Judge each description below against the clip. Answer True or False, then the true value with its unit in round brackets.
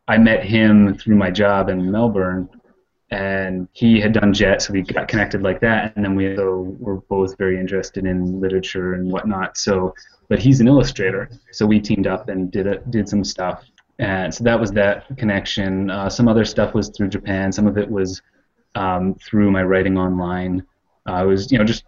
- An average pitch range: False (2.1 semitones)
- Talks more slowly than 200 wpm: False (205 wpm)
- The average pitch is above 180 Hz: False (100 Hz)